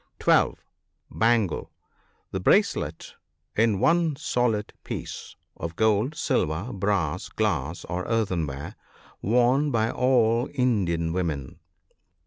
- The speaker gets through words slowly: Yes, slow, 105 wpm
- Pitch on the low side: Yes, low, 105 Hz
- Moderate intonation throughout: No, wide, 6.1 semitones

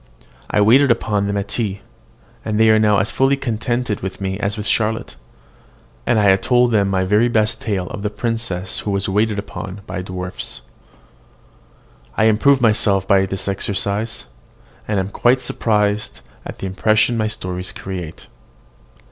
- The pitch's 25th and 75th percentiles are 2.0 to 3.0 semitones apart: Yes, narrow, 2.5 semitones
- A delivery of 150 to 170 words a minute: Yes, average, 160 wpm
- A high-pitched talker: No, low, 105 Hz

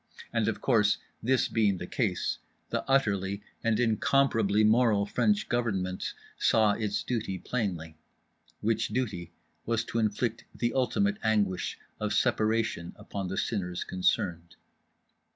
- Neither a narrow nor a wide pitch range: Yes, average, 3.0 semitones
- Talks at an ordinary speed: No, slow, 125 wpm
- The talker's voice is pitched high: No, low, 110 Hz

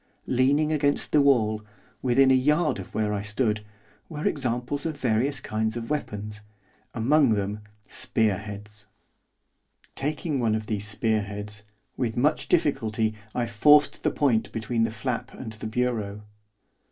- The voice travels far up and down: No, average, 4.3 semitones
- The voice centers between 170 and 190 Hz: No, low, 115 Hz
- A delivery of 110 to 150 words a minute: Yes, average, 145 wpm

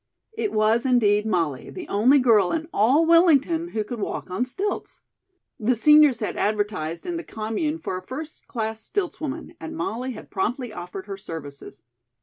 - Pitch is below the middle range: No, high, 235 Hz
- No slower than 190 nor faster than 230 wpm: No, average, 165 wpm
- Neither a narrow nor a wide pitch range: No, wide, 6.9 semitones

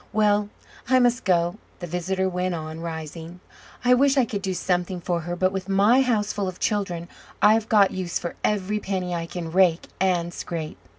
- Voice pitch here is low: No, medium, 185 Hz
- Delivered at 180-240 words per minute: Yes, average, 185 wpm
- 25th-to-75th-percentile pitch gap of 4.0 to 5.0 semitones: No, average, 3.1 semitones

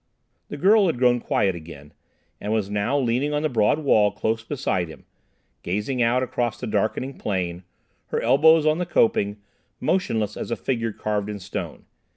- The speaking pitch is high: No, low, 110 Hz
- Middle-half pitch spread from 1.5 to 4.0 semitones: No, average, 5.0 semitones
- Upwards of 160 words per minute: Yes, average, 175 wpm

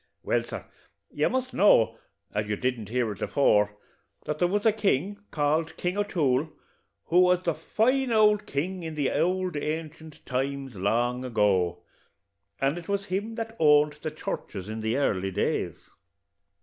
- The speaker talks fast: No, average, 160 wpm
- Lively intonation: Yes, wide, 7.4 semitones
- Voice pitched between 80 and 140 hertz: No, medium, 150 Hz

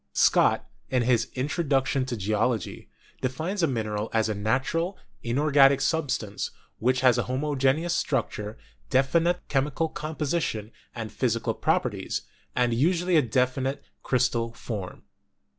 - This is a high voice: No, low, 130 Hz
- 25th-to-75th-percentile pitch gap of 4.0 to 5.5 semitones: Yes, average, 4.5 semitones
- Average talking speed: No, slow, 120 wpm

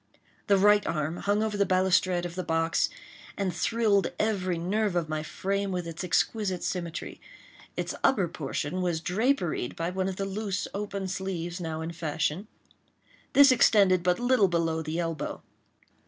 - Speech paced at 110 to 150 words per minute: No, average, 160 wpm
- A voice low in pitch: No, medium, 185 Hz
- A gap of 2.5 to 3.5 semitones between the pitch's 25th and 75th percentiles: Yes, average, 3.2 semitones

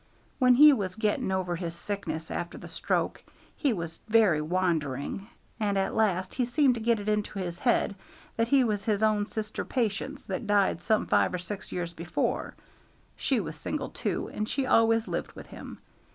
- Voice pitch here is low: No, high, 205 Hz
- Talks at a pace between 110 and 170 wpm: No, average, 185 wpm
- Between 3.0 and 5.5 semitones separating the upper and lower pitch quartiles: Yes, average, 4.2 semitones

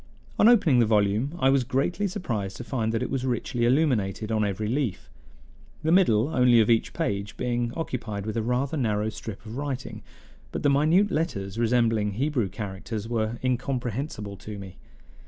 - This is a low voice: Yes, low, 120 Hz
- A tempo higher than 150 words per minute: Yes, average, 175 wpm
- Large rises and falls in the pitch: No, average, 4.3 semitones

